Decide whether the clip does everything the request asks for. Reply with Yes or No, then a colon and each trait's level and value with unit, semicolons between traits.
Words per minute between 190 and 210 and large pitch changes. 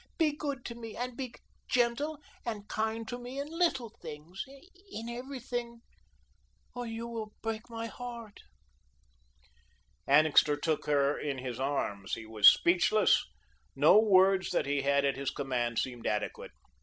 No: average, 145 wpm; wide, 9.0 semitones